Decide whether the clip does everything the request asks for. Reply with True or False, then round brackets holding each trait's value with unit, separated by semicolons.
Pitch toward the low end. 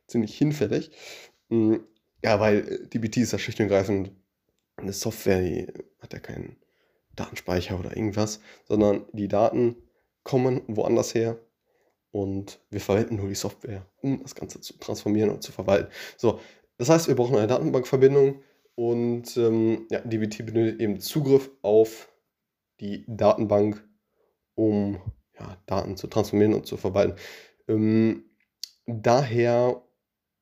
True (110 Hz)